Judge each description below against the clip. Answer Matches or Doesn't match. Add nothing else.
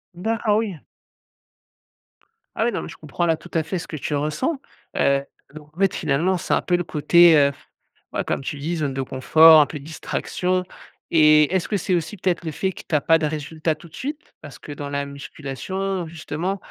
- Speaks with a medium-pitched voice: Matches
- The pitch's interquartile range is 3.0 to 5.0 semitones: Matches